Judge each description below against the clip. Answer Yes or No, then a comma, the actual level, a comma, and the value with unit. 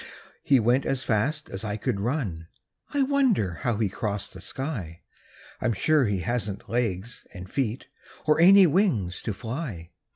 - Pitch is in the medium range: No, low, 115 Hz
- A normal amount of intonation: No, wide, 6.5 semitones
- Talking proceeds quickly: No, average, 160 wpm